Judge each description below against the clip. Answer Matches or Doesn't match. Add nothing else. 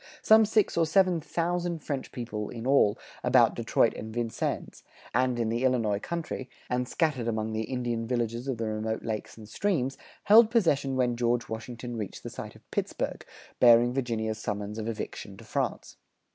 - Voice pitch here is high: Doesn't match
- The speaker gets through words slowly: Doesn't match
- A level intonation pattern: Doesn't match